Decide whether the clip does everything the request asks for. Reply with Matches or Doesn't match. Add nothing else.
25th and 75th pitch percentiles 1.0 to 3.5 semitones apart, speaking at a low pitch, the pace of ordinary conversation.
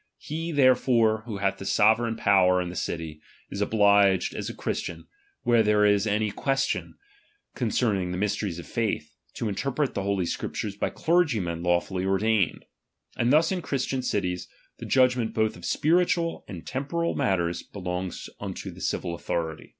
Doesn't match